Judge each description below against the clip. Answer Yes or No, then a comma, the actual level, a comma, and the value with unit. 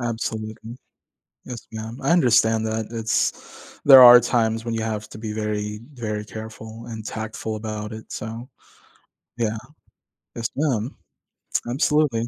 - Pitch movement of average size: No, narrow, 1.5 semitones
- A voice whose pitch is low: Yes, low, 110 Hz